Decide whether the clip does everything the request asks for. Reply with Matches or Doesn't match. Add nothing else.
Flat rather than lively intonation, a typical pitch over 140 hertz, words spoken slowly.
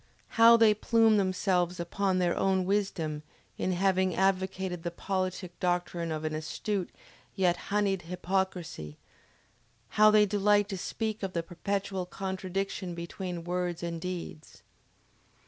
Matches